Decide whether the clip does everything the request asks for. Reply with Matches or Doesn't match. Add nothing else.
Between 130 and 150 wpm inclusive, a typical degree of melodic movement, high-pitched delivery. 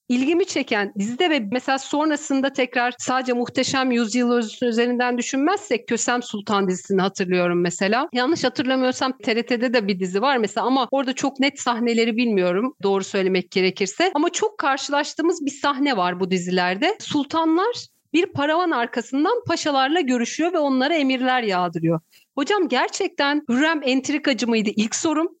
Matches